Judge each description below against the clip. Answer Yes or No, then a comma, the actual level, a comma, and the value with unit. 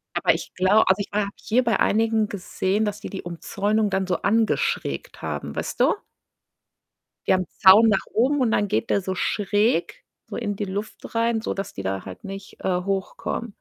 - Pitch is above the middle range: Yes, high, 205 Hz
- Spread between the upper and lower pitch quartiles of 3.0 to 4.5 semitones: No, narrow, 2.6 semitones